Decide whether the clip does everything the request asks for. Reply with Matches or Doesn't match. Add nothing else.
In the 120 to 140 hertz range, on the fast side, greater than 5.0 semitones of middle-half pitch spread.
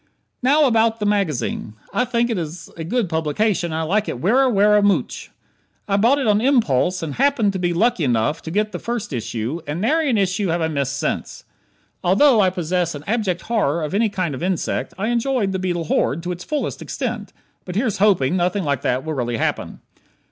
Doesn't match